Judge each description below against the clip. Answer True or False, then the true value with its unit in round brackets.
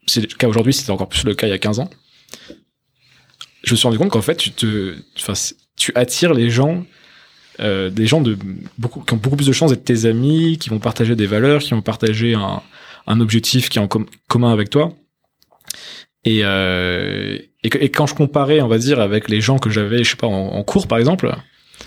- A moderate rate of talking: False (230 wpm)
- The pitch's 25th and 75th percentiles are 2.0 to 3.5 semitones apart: False (4.3 semitones)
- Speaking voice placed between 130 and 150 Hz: False (115 Hz)